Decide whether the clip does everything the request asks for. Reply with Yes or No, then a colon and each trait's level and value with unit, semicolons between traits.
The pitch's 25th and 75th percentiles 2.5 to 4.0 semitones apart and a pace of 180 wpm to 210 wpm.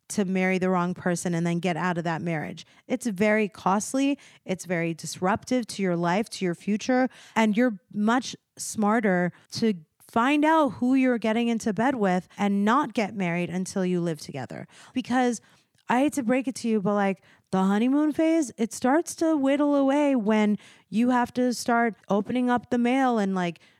No: wide, 5.4 semitones; average, 185 wpm